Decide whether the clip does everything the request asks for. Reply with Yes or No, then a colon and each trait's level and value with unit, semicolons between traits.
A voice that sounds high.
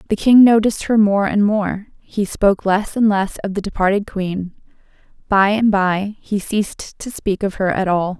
Yes: high, 200 Hz